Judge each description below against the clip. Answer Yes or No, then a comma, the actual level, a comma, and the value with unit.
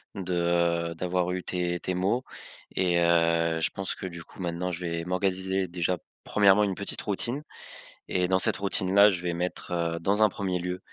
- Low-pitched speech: Yes, very low, 90 Hz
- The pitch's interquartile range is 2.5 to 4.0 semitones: No, narrow, 1.8 semitones